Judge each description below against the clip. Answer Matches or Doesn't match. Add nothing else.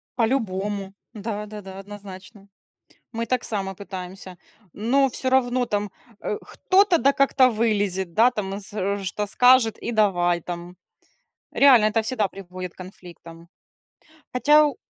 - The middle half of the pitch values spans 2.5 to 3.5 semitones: Doesn't match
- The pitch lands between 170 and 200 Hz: Doesn't match